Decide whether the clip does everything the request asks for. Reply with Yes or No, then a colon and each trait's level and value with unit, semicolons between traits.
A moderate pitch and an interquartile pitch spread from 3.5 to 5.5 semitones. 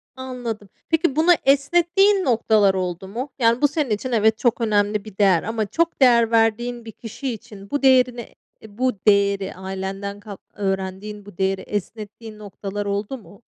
No: high, 220 Hz; average, 3.9 semitones